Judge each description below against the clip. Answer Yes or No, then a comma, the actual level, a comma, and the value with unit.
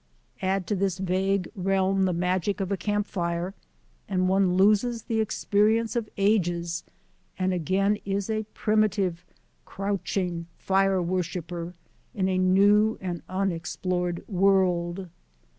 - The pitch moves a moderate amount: No, narrow, 2.0 semitones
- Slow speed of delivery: Yes, slow, 125 wpm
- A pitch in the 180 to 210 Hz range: Yes, high, 190 Hz